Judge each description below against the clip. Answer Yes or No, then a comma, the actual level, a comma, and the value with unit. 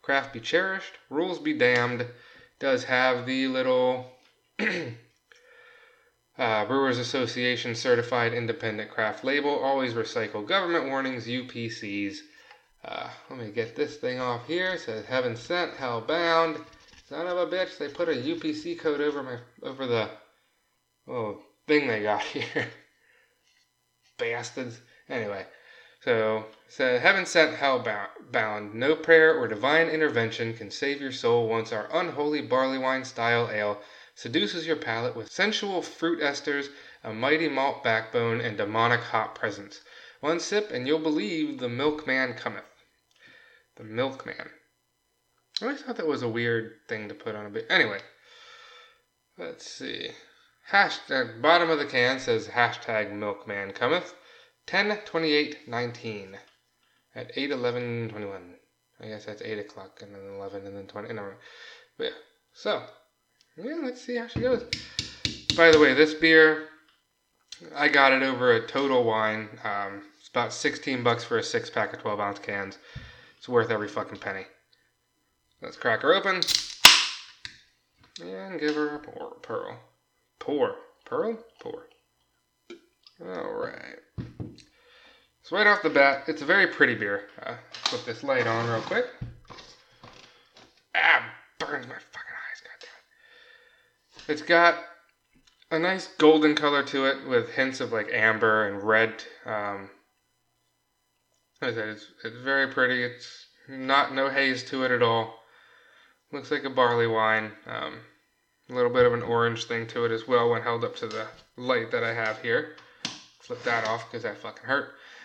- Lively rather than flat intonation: Yes, wide, 6.3 semitones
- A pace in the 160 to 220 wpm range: No, average, 145 wpm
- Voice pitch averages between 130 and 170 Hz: Yes, low, 135 Hz